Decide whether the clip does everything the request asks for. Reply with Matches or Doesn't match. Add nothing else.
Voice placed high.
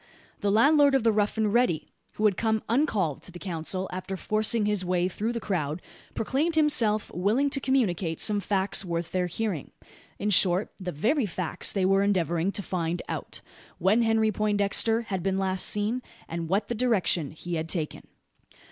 Matches